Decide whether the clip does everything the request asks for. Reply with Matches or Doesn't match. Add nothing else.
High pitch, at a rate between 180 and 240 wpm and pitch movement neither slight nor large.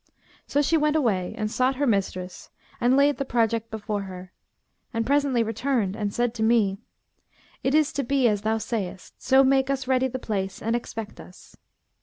Matches